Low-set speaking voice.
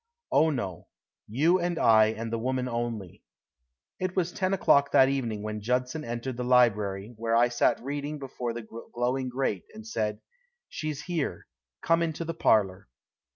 Yes: low, 125 Hz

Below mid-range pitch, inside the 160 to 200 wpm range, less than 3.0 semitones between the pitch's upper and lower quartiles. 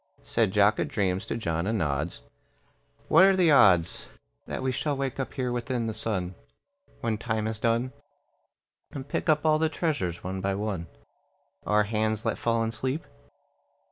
No: low, 110 Hz; average, 170 wpm; average, 5.2 semitones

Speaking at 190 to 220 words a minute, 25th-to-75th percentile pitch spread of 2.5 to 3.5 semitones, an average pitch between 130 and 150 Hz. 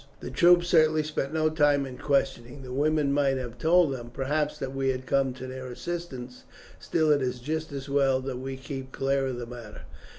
Yes: fast, 205 wpm; average, 2.8 semitones; low, 135 Hz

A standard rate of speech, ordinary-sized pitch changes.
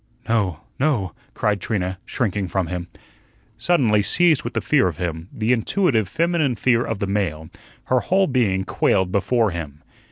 No: average, 160 wpm; wide, 5.8 semitones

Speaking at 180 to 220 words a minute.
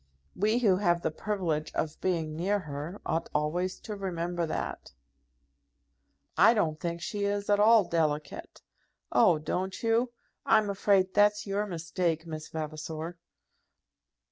No: slow, 135 wpm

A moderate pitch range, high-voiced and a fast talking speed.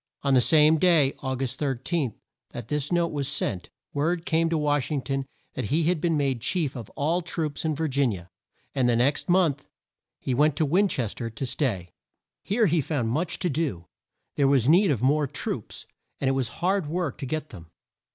No: average, 3.9 semitones; medium, 145 Hz; fast, 215 wpm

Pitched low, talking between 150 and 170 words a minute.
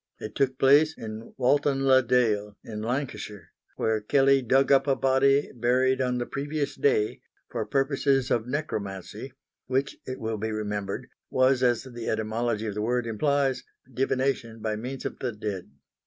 Yes: low, 125 Hz; average, 160 wpm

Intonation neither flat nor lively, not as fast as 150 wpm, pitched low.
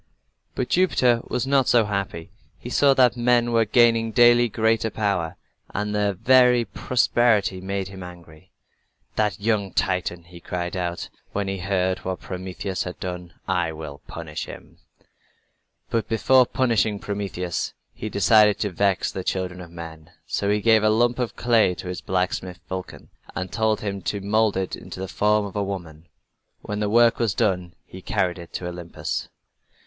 No: average, 3.8 semitones; average, 170 wpm; low, 100 Hz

